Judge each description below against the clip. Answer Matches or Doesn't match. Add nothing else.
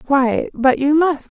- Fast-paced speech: Doesn't match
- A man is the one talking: Doesn't match